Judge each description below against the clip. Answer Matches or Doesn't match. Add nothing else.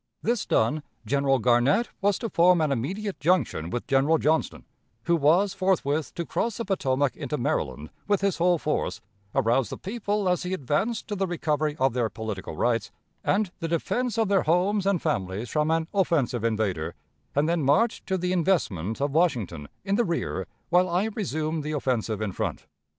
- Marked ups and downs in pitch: Matches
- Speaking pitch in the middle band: Matches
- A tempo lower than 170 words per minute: Doesn't match